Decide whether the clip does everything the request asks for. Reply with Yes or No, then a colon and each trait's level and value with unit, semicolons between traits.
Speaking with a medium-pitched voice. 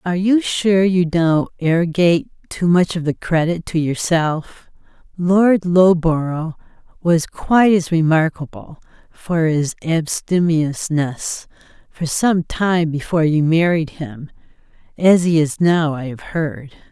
Yes: medium, 165 Hz